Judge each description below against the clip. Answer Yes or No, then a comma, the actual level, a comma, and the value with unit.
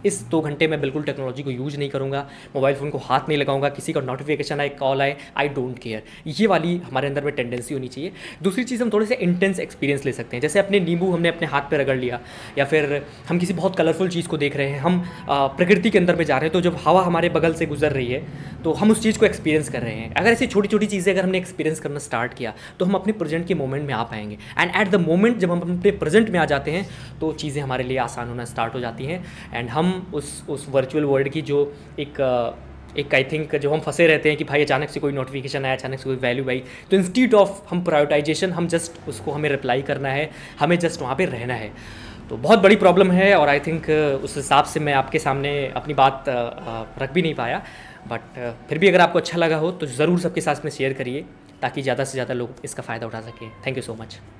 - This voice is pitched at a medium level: Yes, medium, 145 Hz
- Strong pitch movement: No, average, 4.4 semitones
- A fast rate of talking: Yes, fast, 250 wpm